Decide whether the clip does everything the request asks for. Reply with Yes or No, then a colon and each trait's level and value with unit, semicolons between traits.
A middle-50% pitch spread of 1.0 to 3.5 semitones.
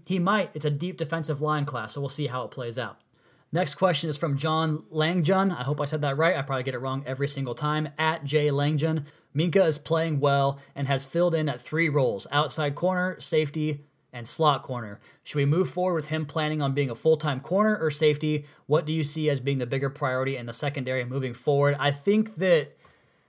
Yes: narrow, 2.5 semitones